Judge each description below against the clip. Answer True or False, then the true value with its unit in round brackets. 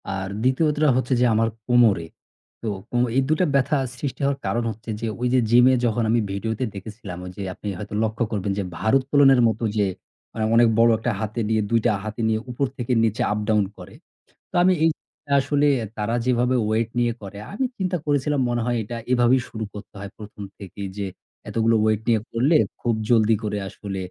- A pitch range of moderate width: True (3.1 semitones)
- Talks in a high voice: False (115 Hz)